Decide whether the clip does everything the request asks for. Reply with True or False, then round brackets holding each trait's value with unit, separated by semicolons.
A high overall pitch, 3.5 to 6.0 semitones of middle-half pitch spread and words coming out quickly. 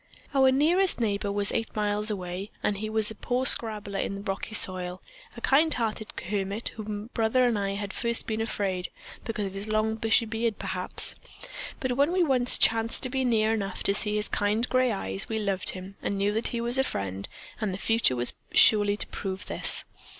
False (215 Hz; 2.8 semitones; 215 wpm)